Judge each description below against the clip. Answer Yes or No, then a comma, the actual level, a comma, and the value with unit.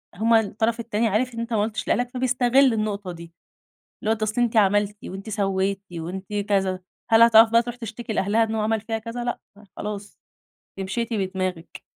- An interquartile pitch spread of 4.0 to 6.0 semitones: No, average, 2.8 semitones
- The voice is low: No, high, 220 Hz